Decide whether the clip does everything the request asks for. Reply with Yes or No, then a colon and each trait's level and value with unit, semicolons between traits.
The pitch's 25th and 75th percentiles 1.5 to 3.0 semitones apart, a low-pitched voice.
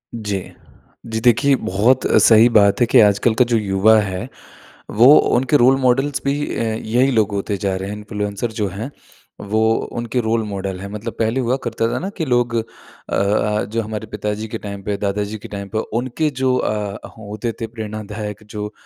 Yes: narrow, 2.6 semitones; low, 110 Hz